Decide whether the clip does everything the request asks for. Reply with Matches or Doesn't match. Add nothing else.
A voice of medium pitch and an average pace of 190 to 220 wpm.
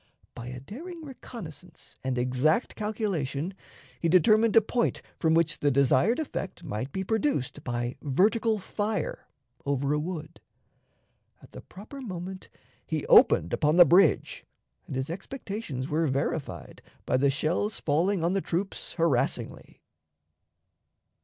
Doesn't match